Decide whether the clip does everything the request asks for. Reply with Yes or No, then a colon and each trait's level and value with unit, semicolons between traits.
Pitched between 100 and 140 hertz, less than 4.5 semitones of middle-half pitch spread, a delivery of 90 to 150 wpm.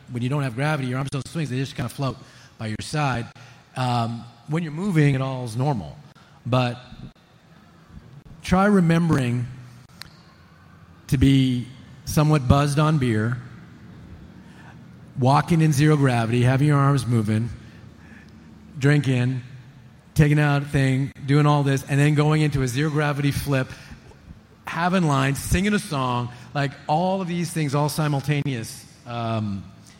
Yes: low, 135 Hz; average, 3.6 semitones; average, 140 wpm